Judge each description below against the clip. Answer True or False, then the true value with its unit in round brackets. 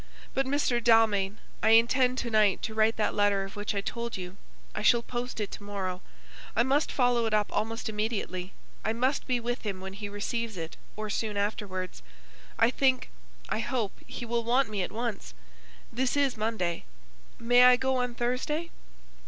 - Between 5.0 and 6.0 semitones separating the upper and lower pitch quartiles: False (3.2 semitones)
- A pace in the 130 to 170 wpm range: False (185 wpm)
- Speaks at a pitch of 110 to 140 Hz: False (225 Hz)